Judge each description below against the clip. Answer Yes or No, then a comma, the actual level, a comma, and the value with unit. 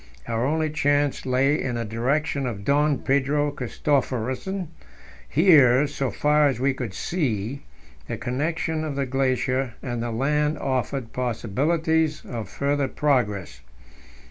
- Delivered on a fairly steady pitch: No, average, 3.2 semitones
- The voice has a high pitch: No, low, 135 Hz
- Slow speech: Yes, slow, 130 wpm